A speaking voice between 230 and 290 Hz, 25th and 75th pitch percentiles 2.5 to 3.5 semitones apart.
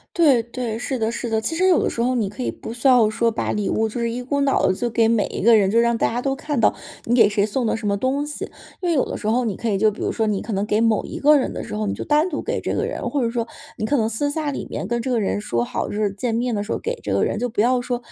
Yes: high, 235 Hz; average, 3.2 semitones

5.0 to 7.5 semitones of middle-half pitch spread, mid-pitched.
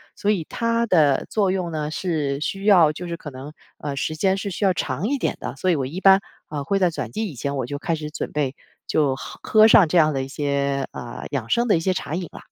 Yes: average, 5.3 semitones; medium, 160 Hz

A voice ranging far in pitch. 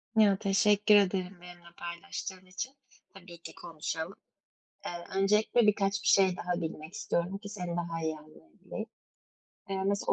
No: average, 2.7 semitones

